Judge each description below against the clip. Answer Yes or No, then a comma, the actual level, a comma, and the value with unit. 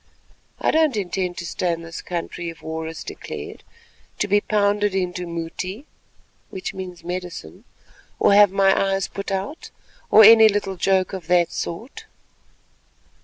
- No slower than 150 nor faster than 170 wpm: No, average, 140 wpm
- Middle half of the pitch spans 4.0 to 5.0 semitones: No, average, 2.9 semitones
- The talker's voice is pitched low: No, high, 190 Hz